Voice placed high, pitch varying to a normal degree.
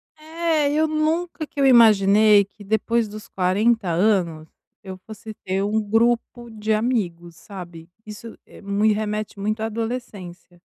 Yes: high, 215 Hz; average, 3.3 semitones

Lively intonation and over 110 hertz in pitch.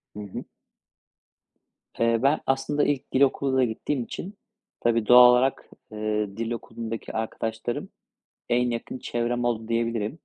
No: narrow, 2.6 semitones; low, 120 Hz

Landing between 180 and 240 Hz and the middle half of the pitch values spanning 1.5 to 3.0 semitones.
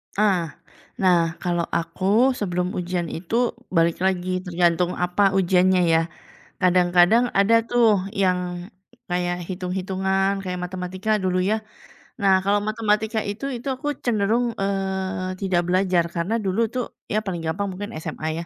Yes: medium, 185 Hz; narrow, 2.6 semitones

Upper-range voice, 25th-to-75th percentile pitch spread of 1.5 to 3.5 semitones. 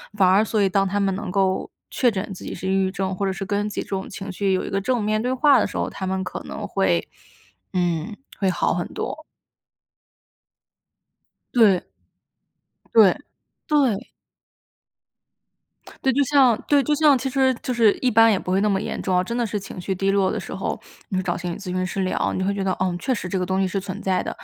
Yes: high, 195 Hz; average, 3.2 semitones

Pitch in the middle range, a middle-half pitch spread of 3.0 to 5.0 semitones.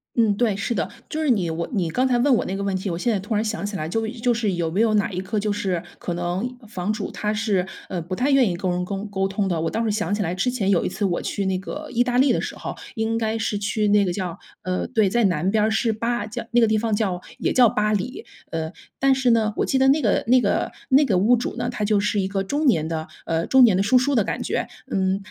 No: high, 210 Hz; average, 3.9 semitones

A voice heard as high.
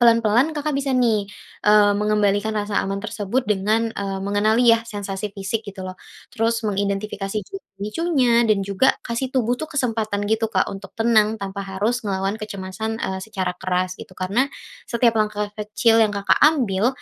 Yes: high, 210 Hz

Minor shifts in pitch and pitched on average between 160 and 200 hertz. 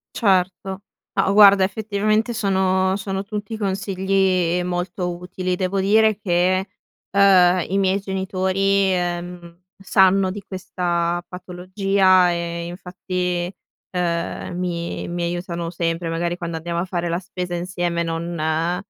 Yes: narrow, 1.8 semitones; medium, 185 Hz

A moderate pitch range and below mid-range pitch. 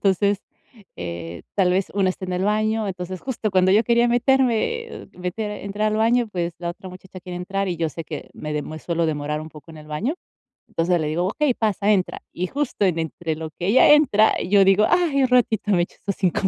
No: average, 4.2 semitones; high, 190 Hz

